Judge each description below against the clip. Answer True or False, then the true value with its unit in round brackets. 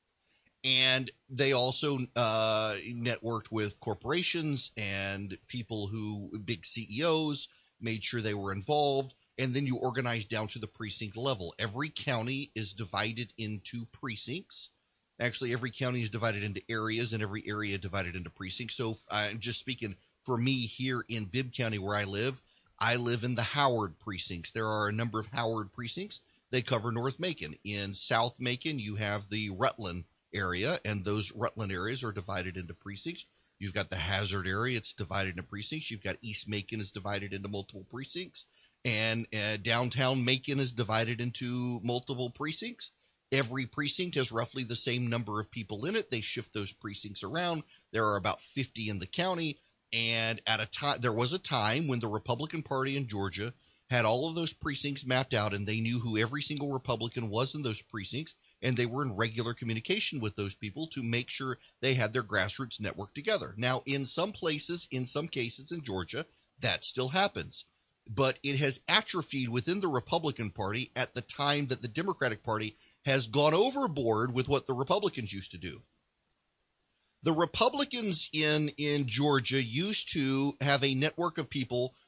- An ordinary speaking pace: True (175 wpm)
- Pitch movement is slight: False (4.2 semitones)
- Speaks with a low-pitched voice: True (120 Hz)